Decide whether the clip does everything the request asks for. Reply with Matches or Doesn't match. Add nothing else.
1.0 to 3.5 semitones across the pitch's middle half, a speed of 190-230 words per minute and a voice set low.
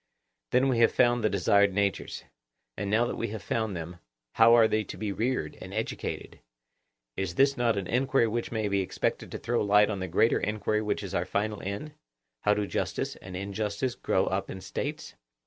Matches